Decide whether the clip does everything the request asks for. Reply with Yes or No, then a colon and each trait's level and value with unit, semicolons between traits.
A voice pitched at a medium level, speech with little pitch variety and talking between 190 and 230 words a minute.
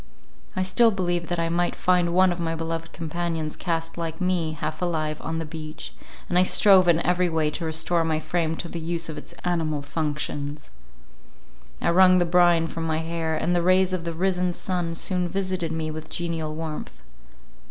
Yes: medium, 170 Hz; narrow, 1.8 semitones; average, 195 wpm